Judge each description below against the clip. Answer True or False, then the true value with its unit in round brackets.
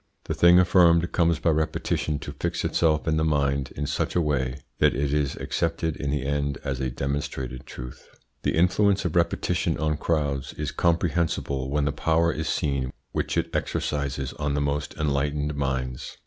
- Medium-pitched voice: False (75 Hz)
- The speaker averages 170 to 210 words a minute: True (175 wpm)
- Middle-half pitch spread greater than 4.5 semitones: False (2.8 semitones)